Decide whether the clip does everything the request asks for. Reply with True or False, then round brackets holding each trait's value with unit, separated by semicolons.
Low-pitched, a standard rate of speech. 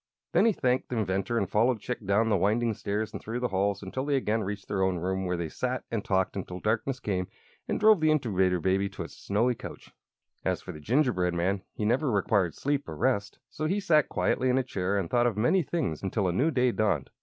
False (110 Hz; 235 wpm)